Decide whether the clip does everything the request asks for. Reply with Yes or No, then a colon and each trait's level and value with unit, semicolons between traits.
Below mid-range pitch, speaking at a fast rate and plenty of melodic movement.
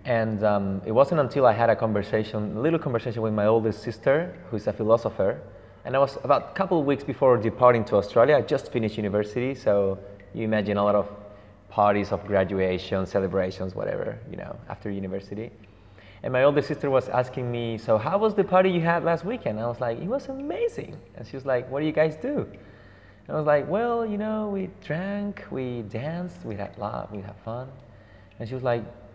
Yes: low, 115 Hz; fast, 215 wpm; wide, 6.2 semitones